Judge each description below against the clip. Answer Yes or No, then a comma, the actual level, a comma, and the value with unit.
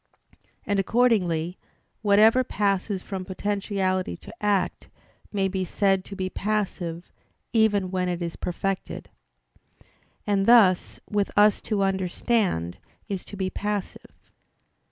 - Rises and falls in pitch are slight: Yes, narrow, 2.0 semitones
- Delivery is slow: Yes, slow, 115 wpm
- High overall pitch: Yes, high, 195 Hz